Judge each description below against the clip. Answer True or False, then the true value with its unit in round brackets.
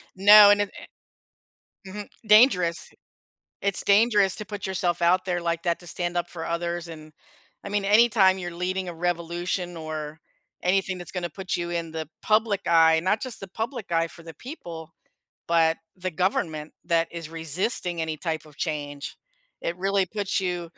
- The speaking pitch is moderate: True (175 Hz)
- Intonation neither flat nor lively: True (3.0 semitones)